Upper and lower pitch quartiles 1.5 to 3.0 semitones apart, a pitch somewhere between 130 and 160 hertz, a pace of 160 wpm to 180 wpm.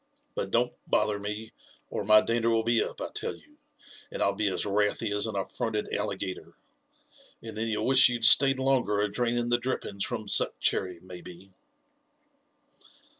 No: average, 2.7 semitones; low, 110 Hz; average, 170 wpm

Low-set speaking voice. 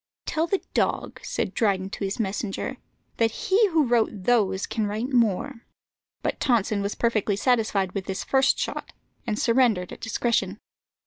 No: high, 225 Hz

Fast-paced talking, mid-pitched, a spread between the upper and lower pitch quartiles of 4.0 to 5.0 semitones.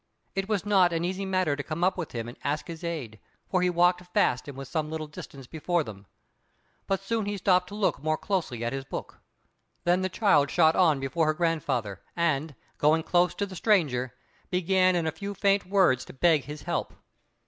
Yes: fast, 210 wpm; medium, 170 Hz; average, 4.5 semitones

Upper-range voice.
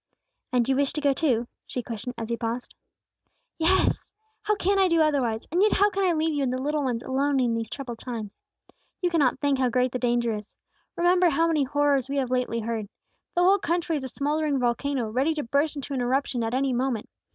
Yes: very high, 270 Hz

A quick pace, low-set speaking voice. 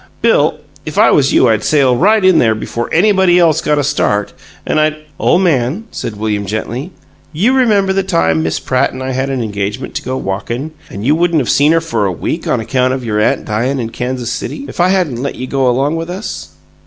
Yes: fast, 230 wpm; low, 130 Hz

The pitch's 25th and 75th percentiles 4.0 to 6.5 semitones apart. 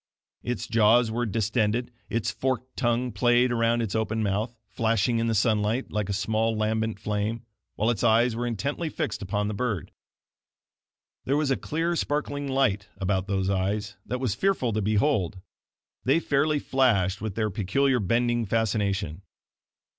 No: average, 3.1 semitones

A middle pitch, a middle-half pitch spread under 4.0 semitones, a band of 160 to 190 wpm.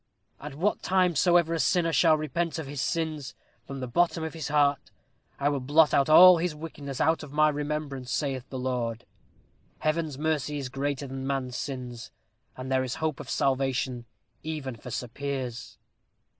Yes: medium, 145 Hz; average, 3.2 semitones; average, 180 wpm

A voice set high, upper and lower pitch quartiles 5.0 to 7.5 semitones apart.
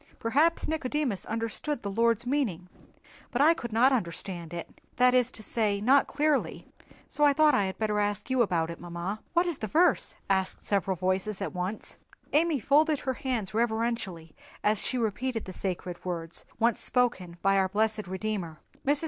Yes: high, 220 Hz; wide, 5.5 semitones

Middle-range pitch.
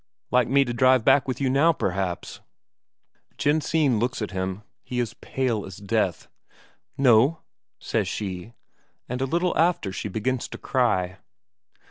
No: low, 125 Hz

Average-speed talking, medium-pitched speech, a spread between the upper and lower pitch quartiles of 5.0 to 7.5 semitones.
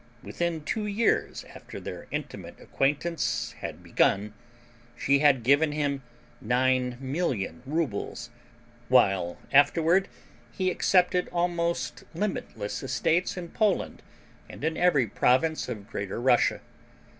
No: slow, 110 wpm; medium, 145 Hz; wide, 5.4 semitones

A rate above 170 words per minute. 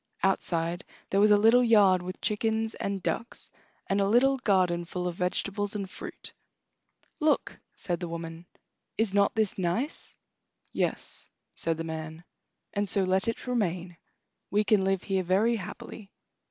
No: average, 155 wpm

